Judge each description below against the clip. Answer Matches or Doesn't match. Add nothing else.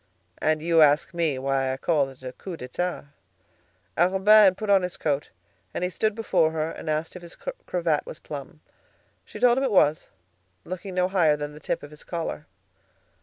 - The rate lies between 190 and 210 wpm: Matches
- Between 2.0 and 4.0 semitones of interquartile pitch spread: Matches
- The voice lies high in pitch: Doesn't match